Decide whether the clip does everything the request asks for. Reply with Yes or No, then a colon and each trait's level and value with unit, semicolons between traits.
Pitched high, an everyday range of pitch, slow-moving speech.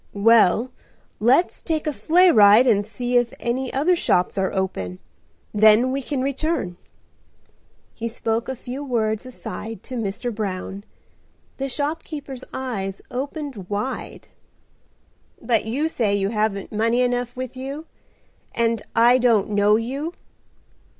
Yes: high, 240 Hz; average, 3.9 semitones; slow, 130 wpm